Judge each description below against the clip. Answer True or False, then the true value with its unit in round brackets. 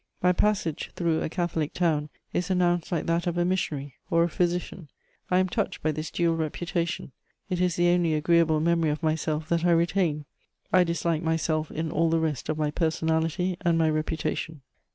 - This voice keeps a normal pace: True (190 wpm)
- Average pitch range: False (1.9 semitones)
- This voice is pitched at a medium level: True (165 Hz)